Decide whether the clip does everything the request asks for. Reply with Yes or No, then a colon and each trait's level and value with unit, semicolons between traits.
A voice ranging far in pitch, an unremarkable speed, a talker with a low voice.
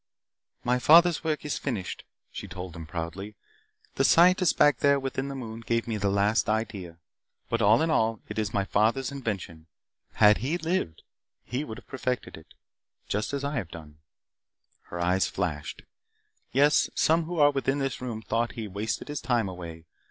Yes: wide, 6.2 semitones; average, 180 wpm; low, 115 Hz